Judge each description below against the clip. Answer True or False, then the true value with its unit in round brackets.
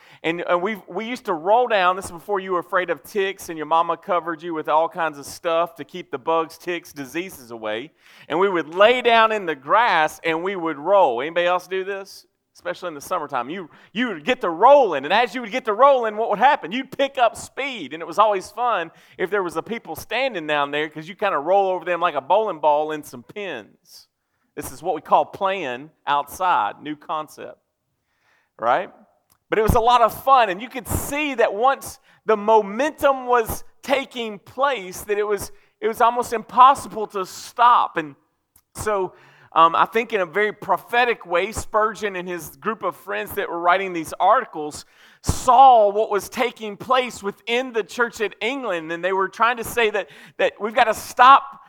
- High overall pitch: True (195 Hz)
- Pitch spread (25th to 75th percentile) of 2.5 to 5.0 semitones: False (5.5 semitones)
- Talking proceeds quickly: True (210 wpm)